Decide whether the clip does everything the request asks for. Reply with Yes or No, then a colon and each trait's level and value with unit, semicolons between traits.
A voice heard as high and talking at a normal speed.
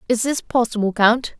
Yes: high, 235 Hz; average, 170 wpm